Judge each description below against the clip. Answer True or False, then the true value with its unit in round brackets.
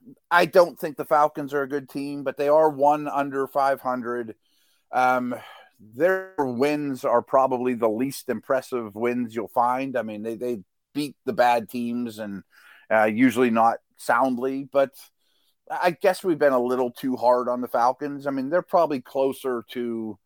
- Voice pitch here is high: False (130 Hz)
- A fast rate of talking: False (170 wpm)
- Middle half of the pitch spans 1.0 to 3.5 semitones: True (3.1 semitones)